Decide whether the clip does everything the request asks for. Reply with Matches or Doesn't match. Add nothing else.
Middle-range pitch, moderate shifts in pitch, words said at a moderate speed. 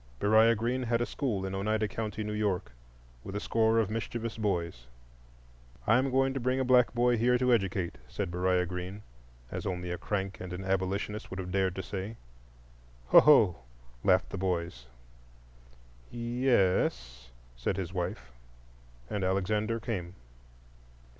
Doesn't match